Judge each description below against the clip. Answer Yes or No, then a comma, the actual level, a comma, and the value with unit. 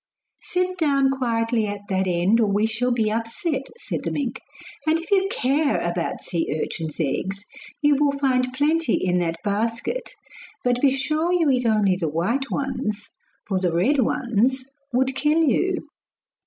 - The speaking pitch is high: Yes, very high, 250 Hz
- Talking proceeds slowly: No, average, 165 wpm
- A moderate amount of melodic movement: No, wide, 5.8 semitones